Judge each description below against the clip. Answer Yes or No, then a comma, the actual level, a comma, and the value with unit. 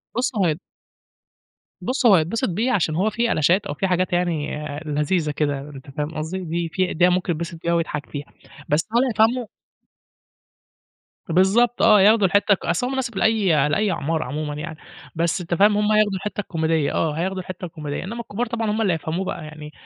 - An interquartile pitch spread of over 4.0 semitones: Yes, average, 5.1 semitones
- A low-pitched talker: No, medium, 180 Hz